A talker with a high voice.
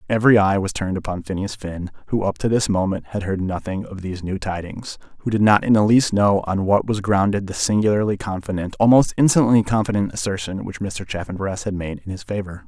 No: low, 100 Hz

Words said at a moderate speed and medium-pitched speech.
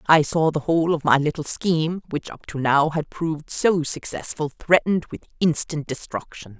Yes: average, 180 wpm; medium, 155 Hz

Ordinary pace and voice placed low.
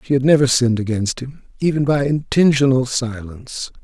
Yes: average, 155 wpm; low, 130 Hz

